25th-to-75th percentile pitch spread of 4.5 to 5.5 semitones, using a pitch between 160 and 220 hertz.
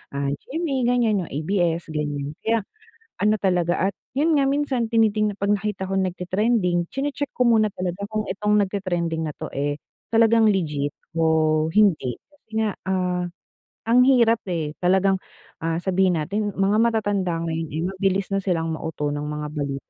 Yes: average, 5.0 semitones; high, 190 Hz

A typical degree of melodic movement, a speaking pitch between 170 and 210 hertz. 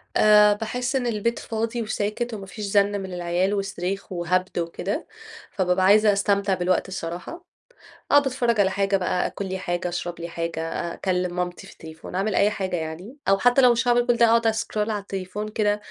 Yes: average, 3.4 semitones; high, 200 Hz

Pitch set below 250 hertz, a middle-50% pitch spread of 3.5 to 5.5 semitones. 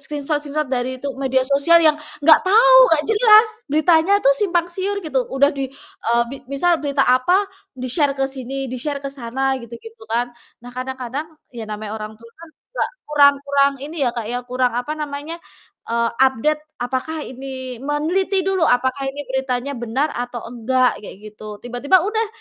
No: very high, 275 Hz; average, 3.8 semitones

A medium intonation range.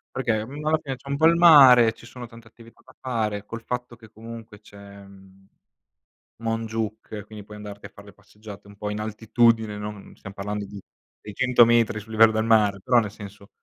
No: narrow, 2.2 semitones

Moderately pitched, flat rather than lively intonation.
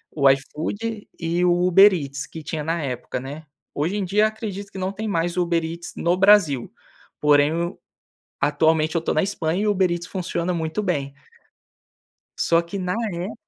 No: medium, 170 Hz; average, 3.5 semitones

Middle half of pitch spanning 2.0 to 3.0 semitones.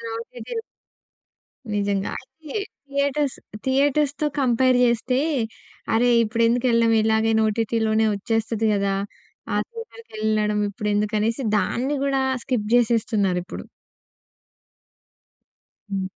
No: average, 3.6 semitones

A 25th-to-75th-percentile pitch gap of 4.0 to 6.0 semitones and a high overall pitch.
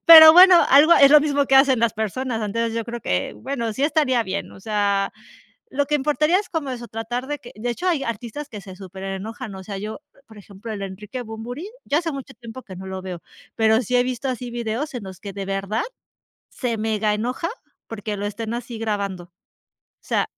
Yes: average, 4.6 semitones; high, 230 Hz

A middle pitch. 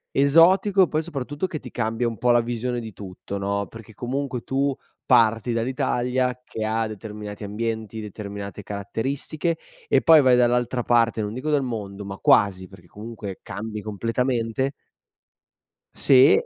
No: low, 115 Hz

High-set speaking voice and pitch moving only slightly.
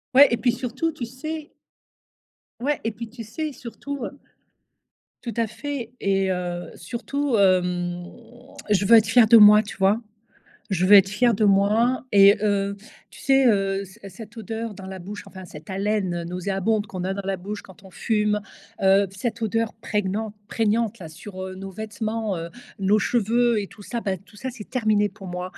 No: high, 210 Hz; average, 3.3 semitones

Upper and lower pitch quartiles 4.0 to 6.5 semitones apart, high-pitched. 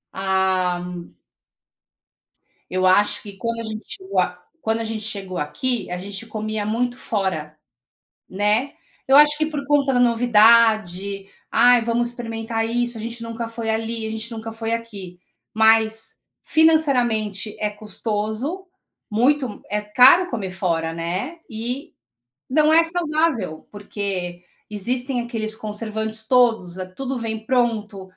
No: average, 3.0 semitones; high, 220 Hz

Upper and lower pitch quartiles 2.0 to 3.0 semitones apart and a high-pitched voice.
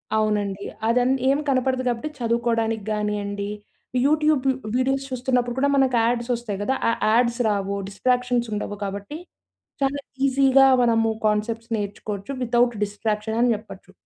No: average, 3.5 semitones; high, 235 Hz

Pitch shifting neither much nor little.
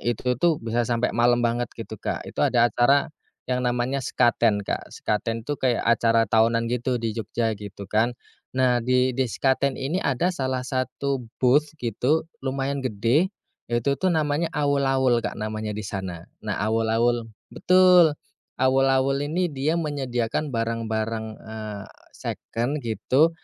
Yes: average, 3.3 semitones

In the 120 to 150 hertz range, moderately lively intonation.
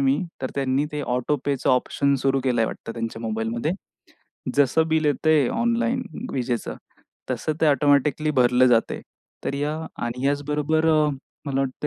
Yes: medium, 140 Hz; average, 3.0 semitones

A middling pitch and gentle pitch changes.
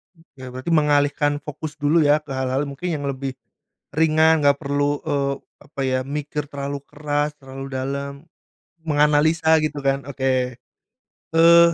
Yes: medium, 145 Hz; narrow, 1.8 semitones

